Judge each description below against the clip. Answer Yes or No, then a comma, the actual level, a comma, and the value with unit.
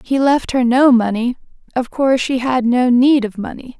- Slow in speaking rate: No, fast, 205 wpm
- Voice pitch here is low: No, very high, 250 Hz